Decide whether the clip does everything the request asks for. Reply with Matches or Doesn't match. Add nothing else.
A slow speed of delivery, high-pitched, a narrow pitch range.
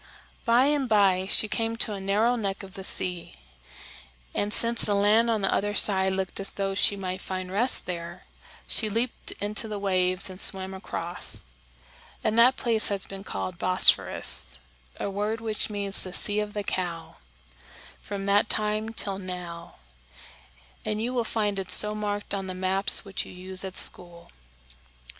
Doesn't match